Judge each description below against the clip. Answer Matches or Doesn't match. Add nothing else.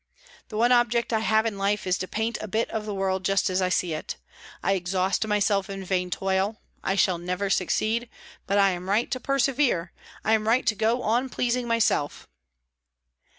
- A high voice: Matches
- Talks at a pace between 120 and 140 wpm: Doesn't match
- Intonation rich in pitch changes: Doesn't match